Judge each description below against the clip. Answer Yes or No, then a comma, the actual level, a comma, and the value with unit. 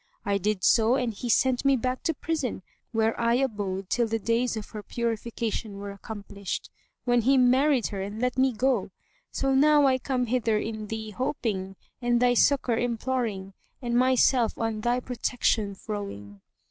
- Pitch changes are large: No, average, 3.1 semitones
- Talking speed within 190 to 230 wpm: No, average, 170 wpm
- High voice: Yes, high, 235 Hz